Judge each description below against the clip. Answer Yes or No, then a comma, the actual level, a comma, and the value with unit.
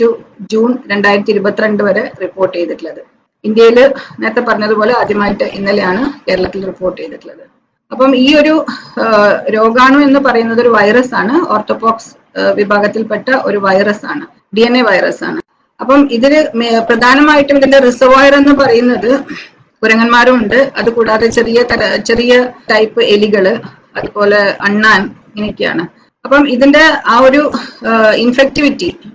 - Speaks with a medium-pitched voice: No, high, 235 Hz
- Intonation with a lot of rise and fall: No, average, 4.1 semitones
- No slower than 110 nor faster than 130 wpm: Yes, average, 115 wpm